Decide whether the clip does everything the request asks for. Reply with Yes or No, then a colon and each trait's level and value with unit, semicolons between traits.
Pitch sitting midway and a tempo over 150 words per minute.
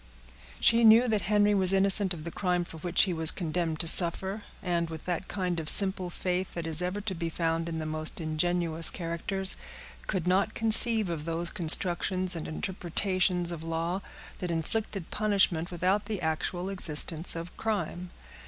Yes: medium, 180 Hz; average, 170 wpm